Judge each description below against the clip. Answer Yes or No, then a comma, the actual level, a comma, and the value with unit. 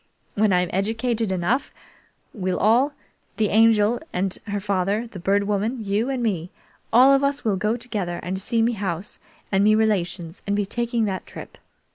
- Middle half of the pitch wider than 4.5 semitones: No, average, 3.2 semitones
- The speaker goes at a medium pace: Yes, average, 175 wpm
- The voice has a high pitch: Yes, high, 210 Hz